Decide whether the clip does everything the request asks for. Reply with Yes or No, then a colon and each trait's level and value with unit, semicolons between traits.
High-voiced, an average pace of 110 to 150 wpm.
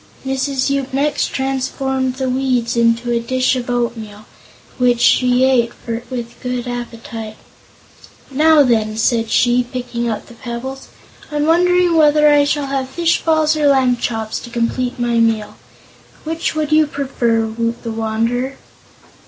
Yes: very high, 250 Hz; average, 145 wpm